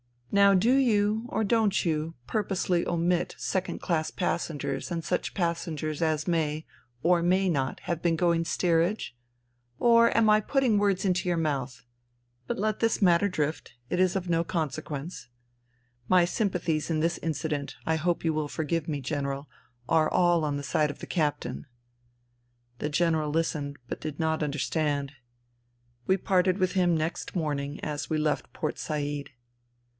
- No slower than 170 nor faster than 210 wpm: No, average, 160 wpm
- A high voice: No, medium, 165 Hz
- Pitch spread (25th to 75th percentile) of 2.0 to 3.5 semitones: Yes, average, 3.2 semitones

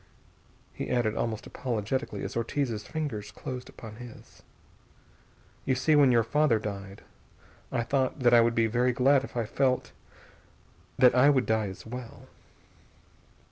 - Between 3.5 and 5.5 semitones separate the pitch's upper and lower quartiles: No, average, 2.9 semitones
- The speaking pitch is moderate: No, low, 120 Hz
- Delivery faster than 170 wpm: No, average, 145 wpm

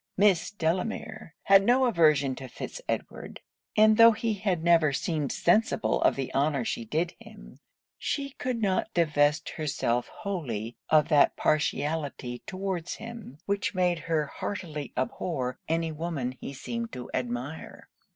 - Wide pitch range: Yes, wide, 6.0 semitones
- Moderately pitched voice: Yes, medium, 165 Hz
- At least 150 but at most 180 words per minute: No, average, 140 wpm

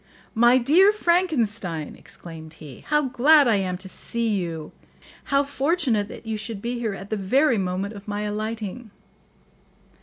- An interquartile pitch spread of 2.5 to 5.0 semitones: No, wide, 5.5 semitones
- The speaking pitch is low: No, high, 220 Hz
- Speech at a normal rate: Yes, average, 155 wpm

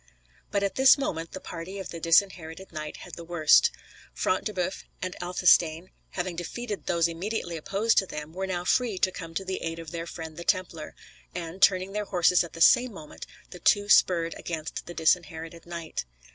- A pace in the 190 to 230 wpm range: Yes, average, 195 wpm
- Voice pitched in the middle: Yes, medium, 175 Hz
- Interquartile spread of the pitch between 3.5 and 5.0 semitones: No, narrow, 2.6 semitones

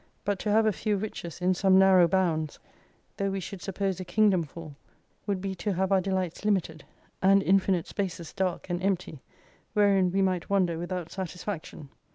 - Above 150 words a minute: Yes, average, 180 wpm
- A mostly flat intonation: Yes, narrow, 2.1 semitones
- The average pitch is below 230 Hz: Yes, high, 190 Hz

